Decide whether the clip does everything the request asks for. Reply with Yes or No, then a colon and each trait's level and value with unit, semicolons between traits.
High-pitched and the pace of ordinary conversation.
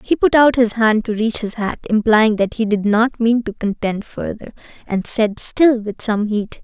No: high, 220 Hz; fast, 215 wpm